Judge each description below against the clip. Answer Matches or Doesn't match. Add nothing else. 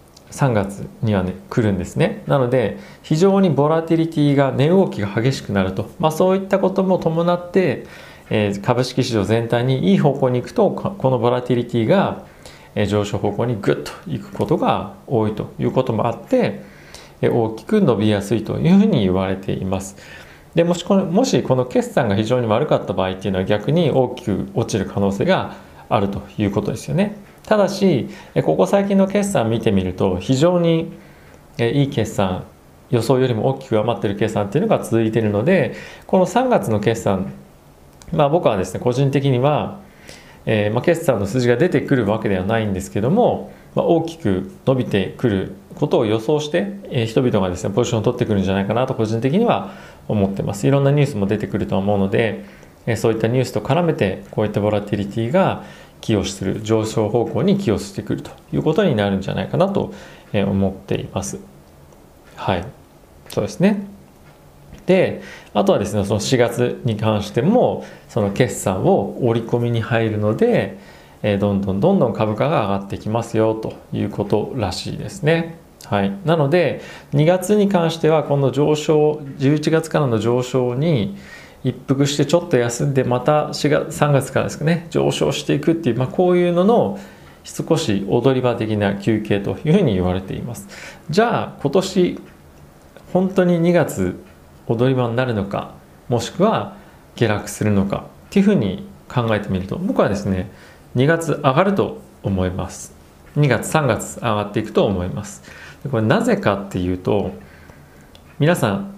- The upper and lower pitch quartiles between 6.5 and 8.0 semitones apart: Matches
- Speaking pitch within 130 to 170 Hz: Doesn't match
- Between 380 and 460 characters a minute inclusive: Doesn't match